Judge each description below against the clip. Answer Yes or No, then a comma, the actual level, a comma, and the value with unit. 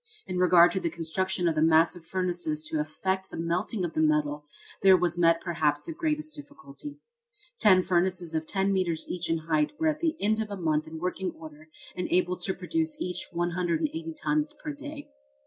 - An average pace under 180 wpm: No, average, 195 wpm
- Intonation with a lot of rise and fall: No, average, 3.8 semitones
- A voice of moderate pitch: Yes, medium, 180 Hz